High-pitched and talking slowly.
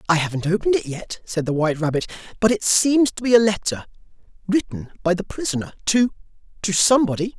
No: high, 195 Hz; average, 180 wpm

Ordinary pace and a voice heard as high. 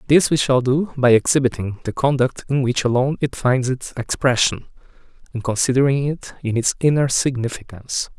No: average, 160 wpm; low, 130 Hz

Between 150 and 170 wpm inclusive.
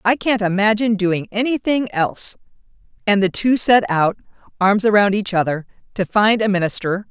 Yes: average, 160 wpm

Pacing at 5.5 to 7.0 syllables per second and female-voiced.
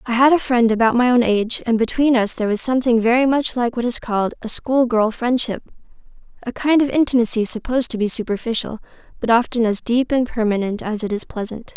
Yes: 6.0 syllables/s; female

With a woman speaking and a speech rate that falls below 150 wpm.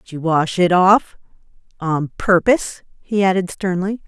Yes: female; slow, 135 wpm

